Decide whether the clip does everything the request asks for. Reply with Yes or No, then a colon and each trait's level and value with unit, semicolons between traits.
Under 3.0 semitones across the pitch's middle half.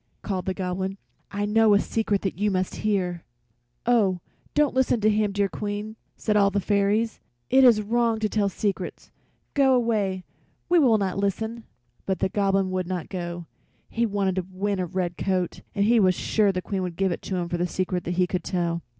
Yes: narrow, 2.6 semitones